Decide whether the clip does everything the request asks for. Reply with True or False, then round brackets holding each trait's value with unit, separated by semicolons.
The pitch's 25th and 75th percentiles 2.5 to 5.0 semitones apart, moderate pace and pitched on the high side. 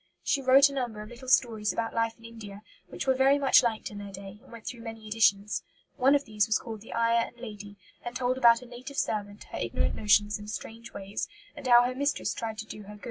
False (3.0 semitones; 245 wpm; 230 Hz)